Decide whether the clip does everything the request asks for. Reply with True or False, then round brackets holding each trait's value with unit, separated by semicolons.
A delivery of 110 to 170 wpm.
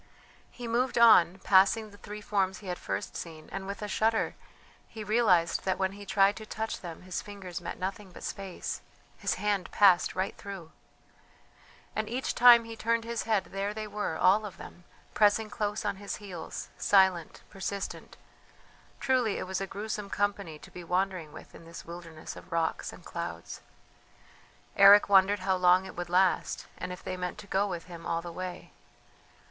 False (185 wpm)